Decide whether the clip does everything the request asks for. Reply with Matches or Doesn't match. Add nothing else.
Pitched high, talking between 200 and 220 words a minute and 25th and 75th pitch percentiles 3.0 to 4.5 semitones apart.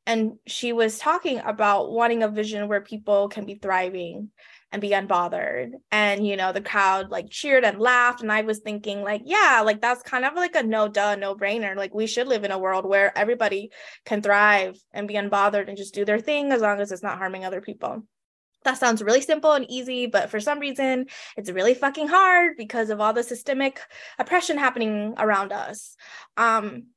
Matches